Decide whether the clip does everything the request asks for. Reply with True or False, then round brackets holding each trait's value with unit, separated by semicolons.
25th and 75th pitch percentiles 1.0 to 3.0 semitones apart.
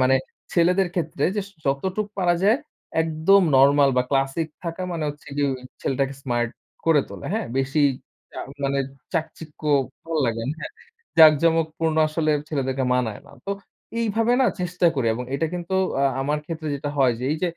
False (3.9 semitones)